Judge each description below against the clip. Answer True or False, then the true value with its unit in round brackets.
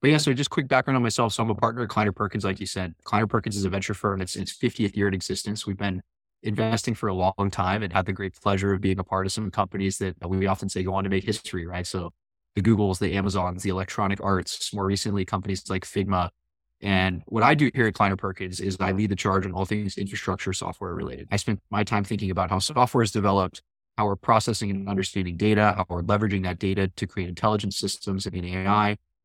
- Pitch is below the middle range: True (100 Hz)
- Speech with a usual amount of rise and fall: False (2.0 semitones)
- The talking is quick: True (245 wpm)